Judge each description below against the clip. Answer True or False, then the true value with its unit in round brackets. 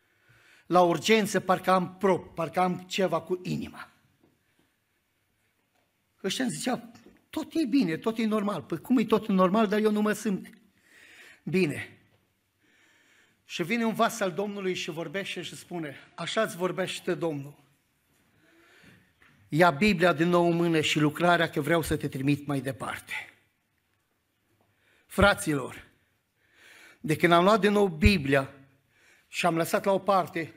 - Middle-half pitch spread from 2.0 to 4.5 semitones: False (5.5 semitones)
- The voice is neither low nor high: True (175 Hz)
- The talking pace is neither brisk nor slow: True (145 wpm)